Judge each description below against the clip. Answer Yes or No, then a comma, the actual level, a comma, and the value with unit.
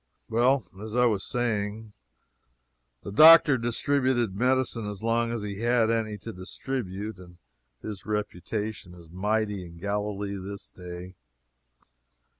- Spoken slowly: Yes, slow, 125 wpm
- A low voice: Yes, low, 105 Hz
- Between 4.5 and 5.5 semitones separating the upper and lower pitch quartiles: No, average, 3.2 semitones